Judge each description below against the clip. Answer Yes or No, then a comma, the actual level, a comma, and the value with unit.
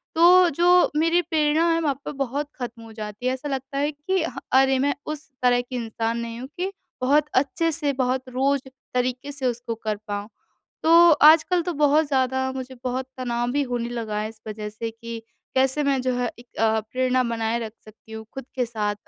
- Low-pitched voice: No, very high, 255 Hz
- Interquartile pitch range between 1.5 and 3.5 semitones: No, average, 4.0 semitones